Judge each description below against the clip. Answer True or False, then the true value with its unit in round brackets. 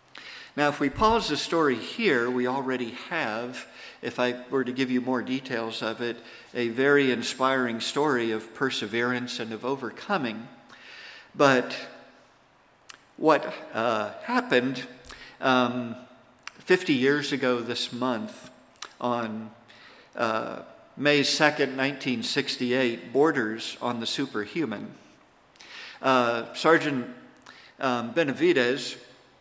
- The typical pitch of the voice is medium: False (125 Hz)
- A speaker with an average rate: False (105 wpm)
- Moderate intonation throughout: False (2.2 semitones)